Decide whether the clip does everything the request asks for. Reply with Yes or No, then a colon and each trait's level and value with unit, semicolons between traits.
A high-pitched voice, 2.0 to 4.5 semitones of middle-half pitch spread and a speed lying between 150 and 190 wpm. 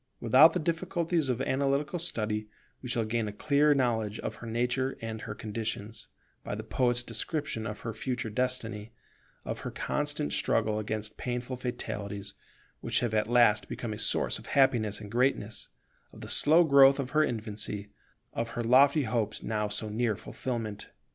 No: low, 120 Hz; average, 3.8 semitones; average, 165 wpm